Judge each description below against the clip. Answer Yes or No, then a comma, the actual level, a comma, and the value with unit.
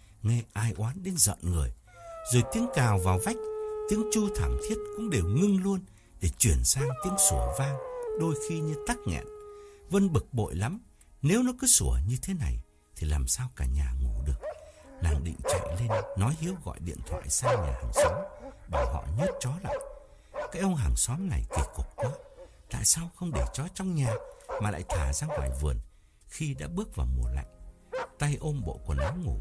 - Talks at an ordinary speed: Yes, average, 200 wpm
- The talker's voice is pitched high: No, low, 115 Hz